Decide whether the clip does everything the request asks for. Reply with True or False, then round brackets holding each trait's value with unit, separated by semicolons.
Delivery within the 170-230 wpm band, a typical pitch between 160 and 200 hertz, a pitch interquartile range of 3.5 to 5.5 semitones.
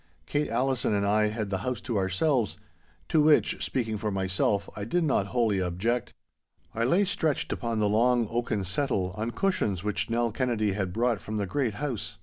False (180 wpm; 110 Hz; 3.8 semitones)